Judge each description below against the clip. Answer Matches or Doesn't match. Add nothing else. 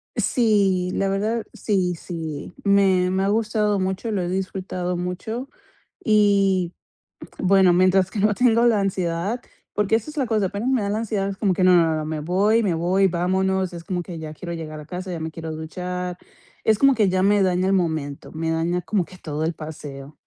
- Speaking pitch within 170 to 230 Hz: Matches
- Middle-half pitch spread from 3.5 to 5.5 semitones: Doesn't match